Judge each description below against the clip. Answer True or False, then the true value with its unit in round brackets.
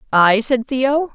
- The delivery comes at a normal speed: True (155 wpm)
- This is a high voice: True (250 Hz)